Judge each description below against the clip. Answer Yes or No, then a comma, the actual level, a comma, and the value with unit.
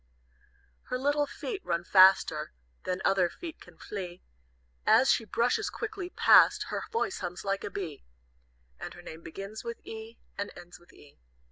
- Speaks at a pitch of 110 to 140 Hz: No, high, 200 Hz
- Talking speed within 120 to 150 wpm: No, average, 160 wpm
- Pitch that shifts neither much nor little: No, wide, 6.5 semitones